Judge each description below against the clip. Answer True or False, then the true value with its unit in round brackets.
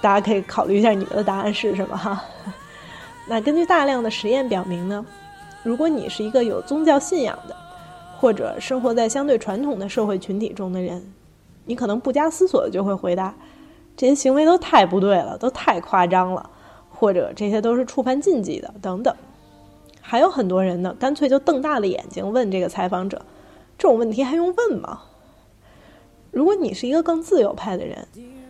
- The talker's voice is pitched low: False (230 Hz)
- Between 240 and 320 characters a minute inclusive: True (285 characters per minute)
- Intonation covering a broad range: True (6.4 semitones)